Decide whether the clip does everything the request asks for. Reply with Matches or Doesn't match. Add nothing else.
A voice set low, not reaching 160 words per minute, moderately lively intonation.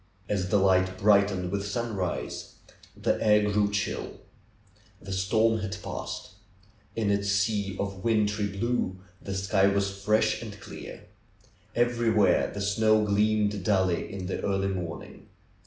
Doesn't match